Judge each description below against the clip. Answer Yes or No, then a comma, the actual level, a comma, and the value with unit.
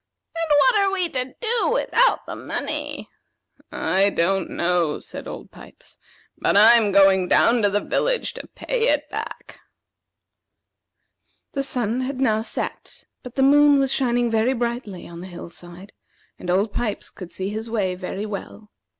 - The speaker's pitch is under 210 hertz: No, high, 225 Hz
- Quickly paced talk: No, average, 160 wpm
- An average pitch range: No, wide, 6.0 semitones